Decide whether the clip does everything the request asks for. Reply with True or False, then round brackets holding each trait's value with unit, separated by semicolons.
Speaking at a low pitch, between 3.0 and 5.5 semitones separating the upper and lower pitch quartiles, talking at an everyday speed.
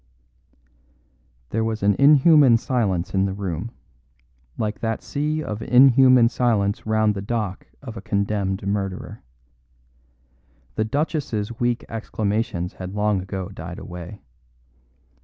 False (105 Hz; 3.5 semitones; 120 wpm)